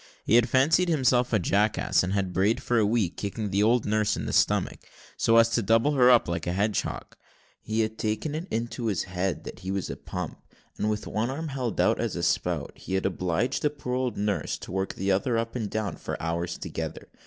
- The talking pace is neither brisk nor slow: No, fast, 230 wpm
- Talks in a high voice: No, low, 110 Hz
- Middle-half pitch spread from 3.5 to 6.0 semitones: Yes, average, 3.9 semitones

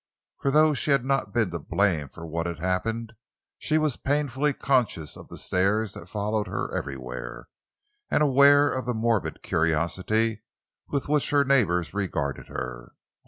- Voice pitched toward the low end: Yes, low, 110 Hz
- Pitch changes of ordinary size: No, wide, 8.1 semitones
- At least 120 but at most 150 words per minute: No, average, 160 wpm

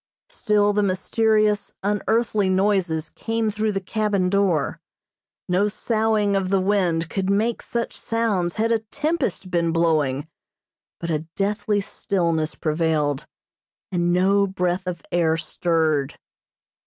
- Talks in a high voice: Yes, high, 195 Hz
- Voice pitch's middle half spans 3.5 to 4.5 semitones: Yes, average, 3.8 semitones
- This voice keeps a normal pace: No, slow, 125 wpm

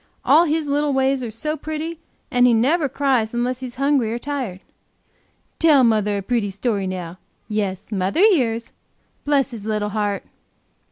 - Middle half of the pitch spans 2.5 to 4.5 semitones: No, average, 5.2 semitones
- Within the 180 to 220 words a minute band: No, average, 160 wpm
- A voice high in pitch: Yes, high, 245 Hz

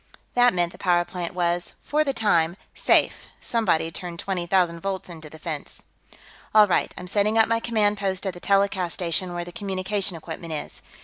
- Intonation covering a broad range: No, average, 2.9 semitones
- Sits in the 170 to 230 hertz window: Yes, medium, 185 Hz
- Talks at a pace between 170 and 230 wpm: Yes, average, 190 wpm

